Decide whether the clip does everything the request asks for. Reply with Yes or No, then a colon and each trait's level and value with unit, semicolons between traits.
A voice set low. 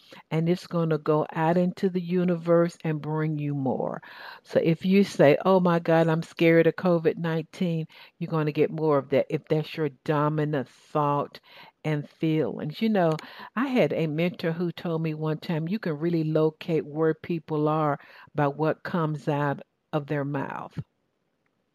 No: medium, 160 Hz